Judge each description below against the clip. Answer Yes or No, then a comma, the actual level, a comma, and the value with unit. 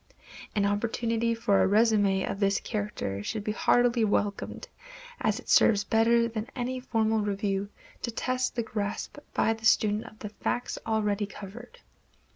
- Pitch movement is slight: Yes, narrow, 2.3 semitones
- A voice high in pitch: Yes, high, 215 Hz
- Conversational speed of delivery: Yes, average, 155 wpm